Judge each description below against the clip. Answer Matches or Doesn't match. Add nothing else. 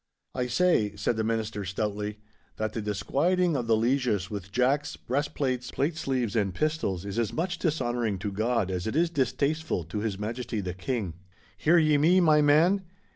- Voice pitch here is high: Doesn't match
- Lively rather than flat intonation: Matches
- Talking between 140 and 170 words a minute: Doesn't match